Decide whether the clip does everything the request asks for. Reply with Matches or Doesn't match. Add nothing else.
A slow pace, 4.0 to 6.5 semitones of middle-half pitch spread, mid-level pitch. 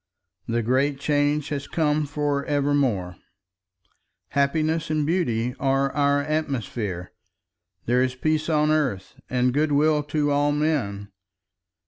Doesn't match